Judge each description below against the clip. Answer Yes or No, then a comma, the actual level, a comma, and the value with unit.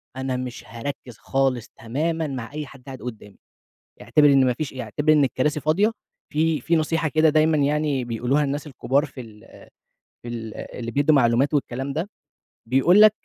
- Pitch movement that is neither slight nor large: Yes, average, 3.7 semitones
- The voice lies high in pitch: No, medium, 140 Hz